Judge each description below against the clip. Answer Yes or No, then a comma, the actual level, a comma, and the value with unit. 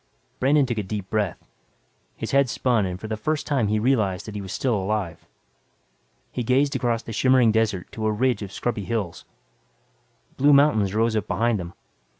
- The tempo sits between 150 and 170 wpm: No, average, 185 wpm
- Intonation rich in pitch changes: No, average, 3.9 semitones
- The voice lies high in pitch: No, low, 110 Hz